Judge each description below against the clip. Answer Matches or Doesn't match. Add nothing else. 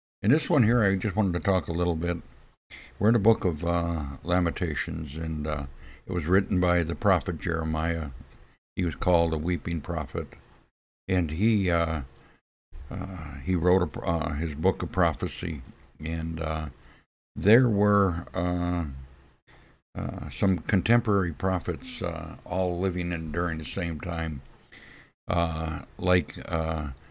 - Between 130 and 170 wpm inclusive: Matches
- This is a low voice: Matches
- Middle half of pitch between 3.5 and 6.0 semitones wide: Doesn't match